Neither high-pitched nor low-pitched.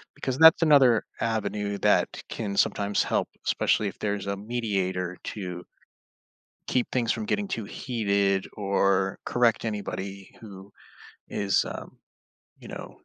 No: low, 100 Hz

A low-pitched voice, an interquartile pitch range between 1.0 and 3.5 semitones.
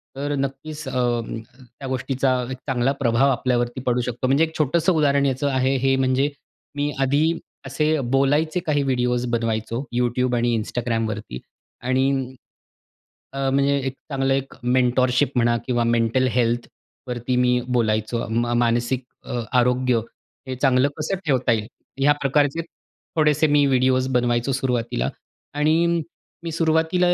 Yes: low, 130 Hz; average, 2.7 semitones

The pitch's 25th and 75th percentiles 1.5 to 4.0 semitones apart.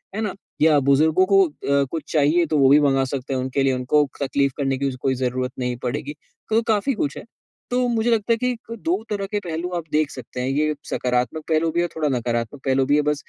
No: average, 4.5 semitones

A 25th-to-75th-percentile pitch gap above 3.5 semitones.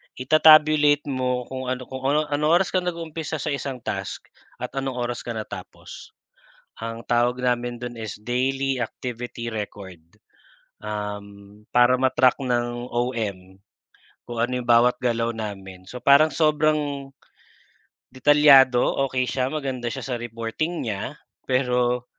No: average, 3.0 semitones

